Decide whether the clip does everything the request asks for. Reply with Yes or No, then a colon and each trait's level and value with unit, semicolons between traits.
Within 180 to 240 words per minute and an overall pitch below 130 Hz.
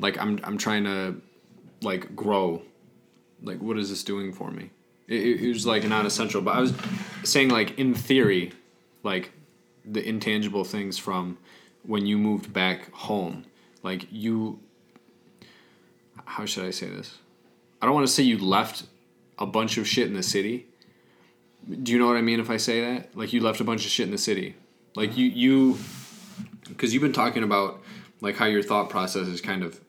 Yes: average, 190 wpm; low, 110 Hz